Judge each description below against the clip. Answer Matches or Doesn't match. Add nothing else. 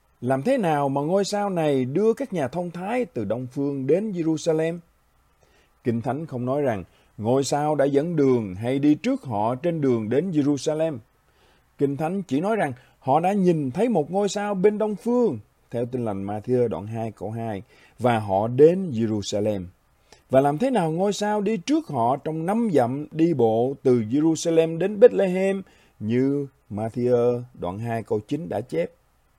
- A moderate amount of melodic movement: Doesn't match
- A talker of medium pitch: Matches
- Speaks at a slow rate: Doesn't match